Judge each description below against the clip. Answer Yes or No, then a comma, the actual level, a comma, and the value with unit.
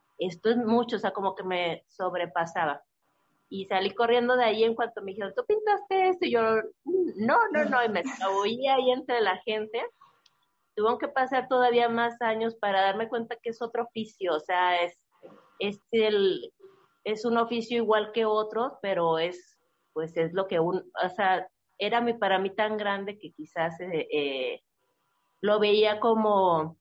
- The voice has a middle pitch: No, high, 215 Hz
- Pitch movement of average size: Yes, average, 4.3 semitones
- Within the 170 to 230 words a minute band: Yes, average, 175 wpm